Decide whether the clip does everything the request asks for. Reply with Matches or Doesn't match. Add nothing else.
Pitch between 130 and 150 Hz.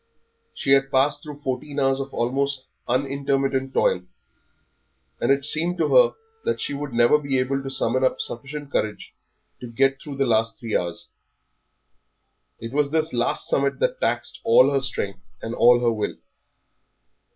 Matches